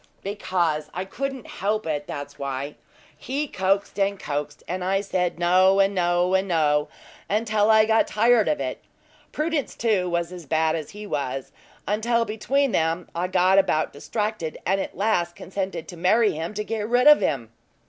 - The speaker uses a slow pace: No, average, 175 wpm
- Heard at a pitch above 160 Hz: Yes, high, 190 Hz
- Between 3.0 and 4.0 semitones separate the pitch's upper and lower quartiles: No, average, 4.6 semitones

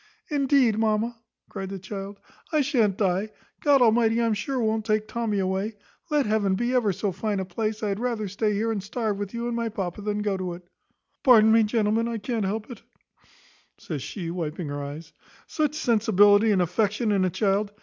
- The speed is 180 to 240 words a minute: Yes, average, 200 wpm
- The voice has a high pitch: Yes, high, 215 Hz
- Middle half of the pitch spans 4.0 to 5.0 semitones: No, average, 2.8 semitones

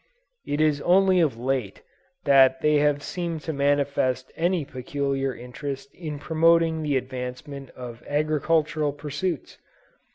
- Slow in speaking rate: Yes, slow, 125 wpm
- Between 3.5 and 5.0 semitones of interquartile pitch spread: No, average, 2.8 semitones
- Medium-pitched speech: Yes, medium, 145 Hz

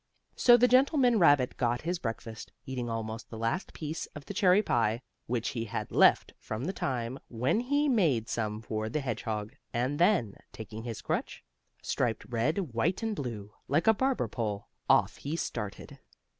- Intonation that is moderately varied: No, wide, 8.0 semitones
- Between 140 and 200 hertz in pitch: No, low, 125 Hz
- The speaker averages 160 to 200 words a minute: Yes, average, 175 wpm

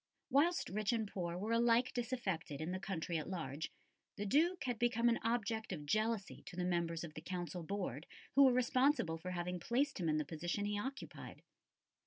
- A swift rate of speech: No, average, 195 wpm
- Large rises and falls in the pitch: Yes, wide, 5.7 semitones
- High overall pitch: Yes, high, 200 Hz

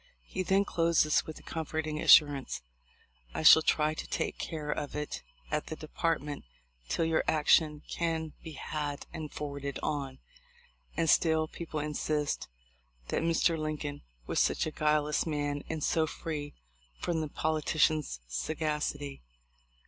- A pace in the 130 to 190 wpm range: Yes, average, 140 wpm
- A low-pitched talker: No, medium, 155 Hz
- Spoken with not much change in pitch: Yes, narrow, 1.5 semitones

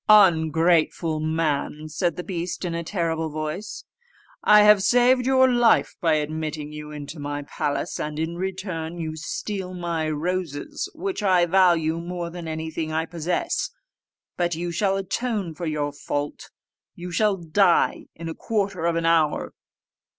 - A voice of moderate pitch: Yes, medium, 170 Hz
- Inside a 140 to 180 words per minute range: Yes, average, 150 wpm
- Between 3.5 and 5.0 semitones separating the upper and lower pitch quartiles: No, average, 3.1 semitones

